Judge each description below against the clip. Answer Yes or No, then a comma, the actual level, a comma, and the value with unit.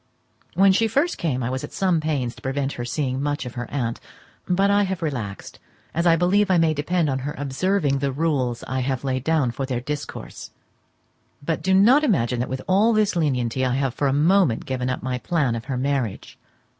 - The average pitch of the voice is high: No, medium, 140 Hz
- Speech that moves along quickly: Yes, fast, 215 wpm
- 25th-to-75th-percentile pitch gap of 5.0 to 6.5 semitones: Yes, wide, 5.6 semitones